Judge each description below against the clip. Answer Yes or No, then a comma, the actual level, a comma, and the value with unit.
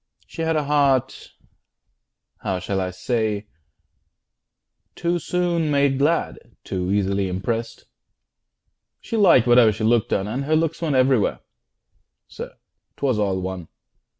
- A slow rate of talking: Yes, slow, 125 wpm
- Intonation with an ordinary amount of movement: No, wide, 7.0 semitones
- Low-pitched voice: Yes, low, 120 Hz